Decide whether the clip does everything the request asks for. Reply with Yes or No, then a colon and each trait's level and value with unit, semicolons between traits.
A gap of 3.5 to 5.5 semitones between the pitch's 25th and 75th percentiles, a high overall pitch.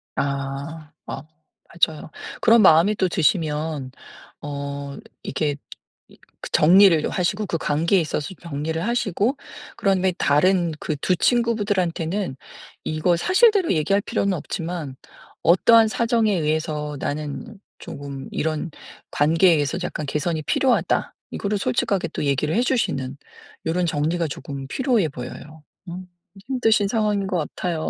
No: average, 5.1 semitones; medium, 165 Hz